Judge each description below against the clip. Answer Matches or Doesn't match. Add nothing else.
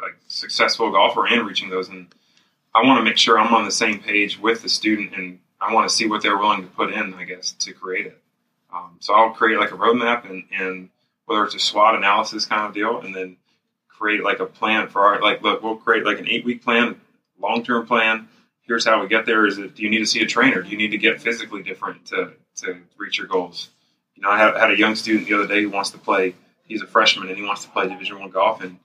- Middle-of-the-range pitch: Doesn't match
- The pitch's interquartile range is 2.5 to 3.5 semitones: Matches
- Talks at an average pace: Doesn't match